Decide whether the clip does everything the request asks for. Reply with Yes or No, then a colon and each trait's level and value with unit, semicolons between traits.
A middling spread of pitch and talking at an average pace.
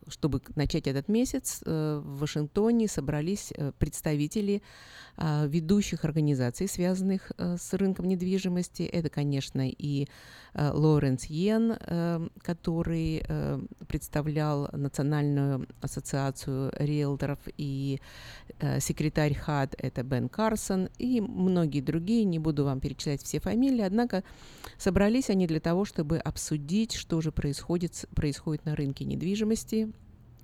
No: average, 4.7 semitones; slow, 105 wpm